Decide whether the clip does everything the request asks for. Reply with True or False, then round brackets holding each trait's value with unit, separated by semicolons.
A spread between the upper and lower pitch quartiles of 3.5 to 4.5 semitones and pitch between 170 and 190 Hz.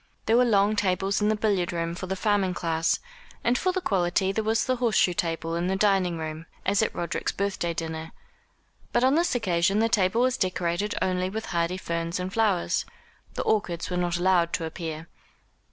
True (3.9 semitones; 185 Hz)